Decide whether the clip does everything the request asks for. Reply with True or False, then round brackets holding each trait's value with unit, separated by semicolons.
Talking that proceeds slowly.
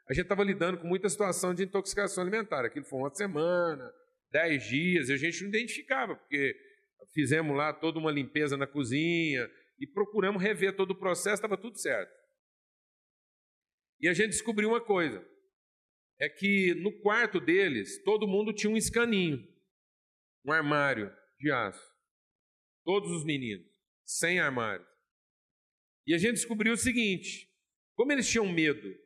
False (150 wpm)